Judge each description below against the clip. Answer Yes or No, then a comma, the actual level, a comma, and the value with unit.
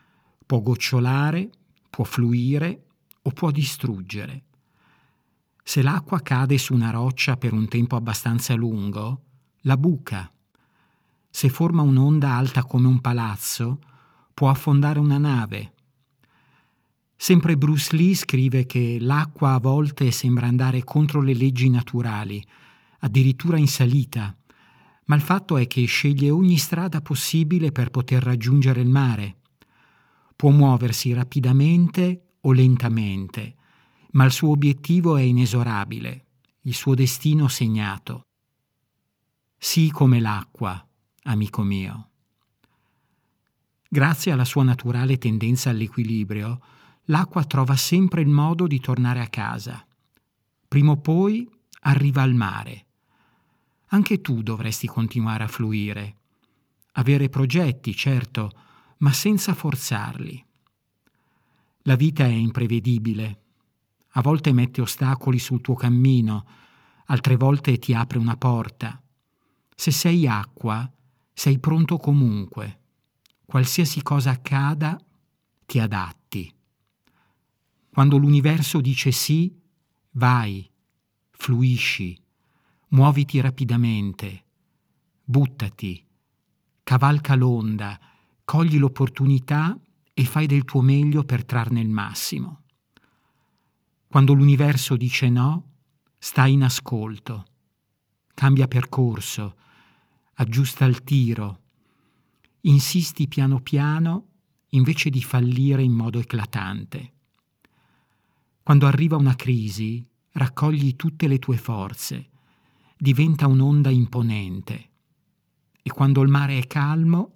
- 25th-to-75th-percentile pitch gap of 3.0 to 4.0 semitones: Yes, average, 3.4 semitones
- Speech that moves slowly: Yes, slow, 105 wpm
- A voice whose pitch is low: Yes, low, 130 Hz